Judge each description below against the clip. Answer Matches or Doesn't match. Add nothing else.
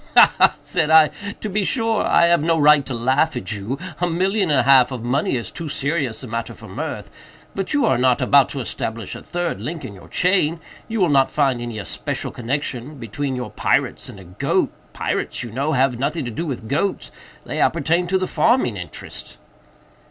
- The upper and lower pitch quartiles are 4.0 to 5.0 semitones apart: Doesn't match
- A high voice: Doesn't match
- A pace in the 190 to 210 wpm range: Matches